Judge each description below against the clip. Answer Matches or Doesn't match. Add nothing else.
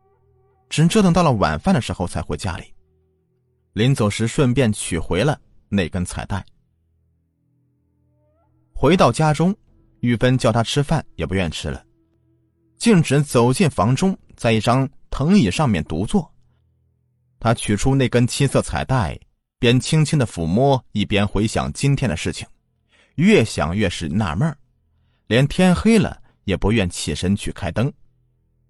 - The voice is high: Doesn't match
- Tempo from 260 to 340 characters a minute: Doesn't match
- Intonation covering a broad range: Matches